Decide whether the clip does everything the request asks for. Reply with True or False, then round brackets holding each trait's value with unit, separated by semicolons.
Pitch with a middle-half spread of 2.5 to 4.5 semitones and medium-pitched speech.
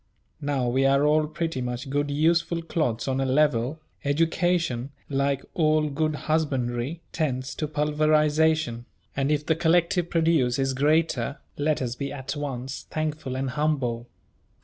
True (3.0 semitones; 145 Hz)